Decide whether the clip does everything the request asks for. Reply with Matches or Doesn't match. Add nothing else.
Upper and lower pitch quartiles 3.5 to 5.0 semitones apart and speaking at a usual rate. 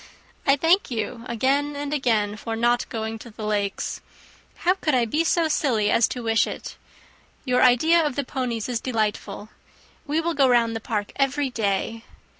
Matches